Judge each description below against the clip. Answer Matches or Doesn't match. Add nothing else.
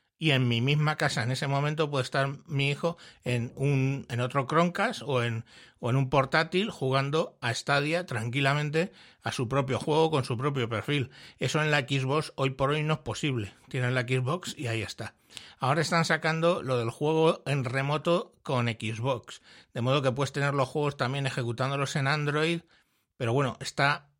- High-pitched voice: Doesn't match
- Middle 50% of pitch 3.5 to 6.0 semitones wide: Doesn't match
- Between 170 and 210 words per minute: Matches